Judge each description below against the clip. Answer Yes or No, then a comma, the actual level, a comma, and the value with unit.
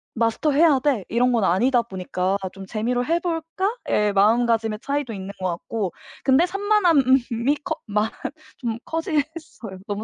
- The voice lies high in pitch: Yes, high, 240 Hz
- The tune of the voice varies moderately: No, wide, 6.4 semitones